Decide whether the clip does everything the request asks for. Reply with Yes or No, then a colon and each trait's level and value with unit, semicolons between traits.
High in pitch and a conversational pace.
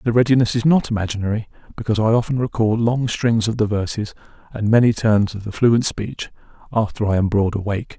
No: low, 110 Hz; average, 195 wpm